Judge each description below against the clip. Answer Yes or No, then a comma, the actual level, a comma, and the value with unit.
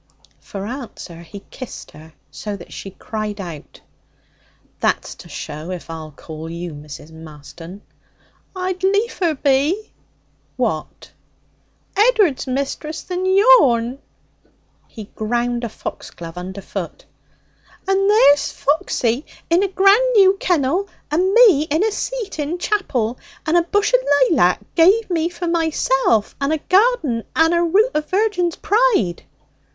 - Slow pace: Yes, slow, 130 wpm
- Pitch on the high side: Yes, very high, 295 Hz